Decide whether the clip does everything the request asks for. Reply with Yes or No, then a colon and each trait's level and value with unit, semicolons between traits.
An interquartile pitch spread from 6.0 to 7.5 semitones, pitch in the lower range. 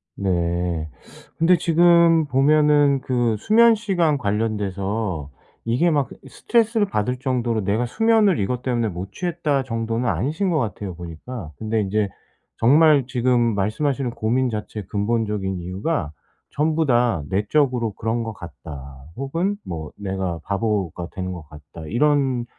Yes: wide, 7.0 semitones; low, 115 Hz